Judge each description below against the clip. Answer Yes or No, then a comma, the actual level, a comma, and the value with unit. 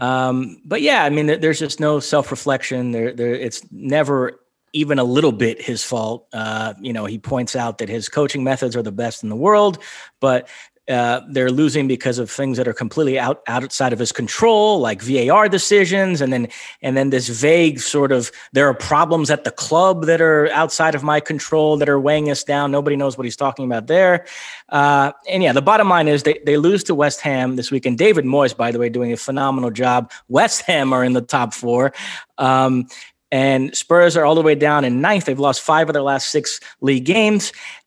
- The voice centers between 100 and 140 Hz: Yes, low, 135 Hz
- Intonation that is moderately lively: Yes, average, 3.4 semitones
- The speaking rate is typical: No, fast, 215 wpm